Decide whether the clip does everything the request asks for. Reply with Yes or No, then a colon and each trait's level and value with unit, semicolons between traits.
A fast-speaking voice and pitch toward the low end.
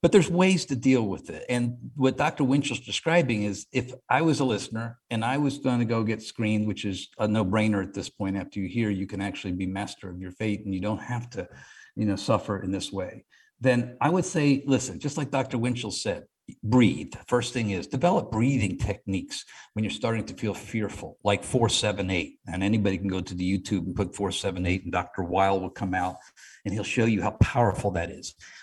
Yes: fast, 225 wpm; low, 110 Hz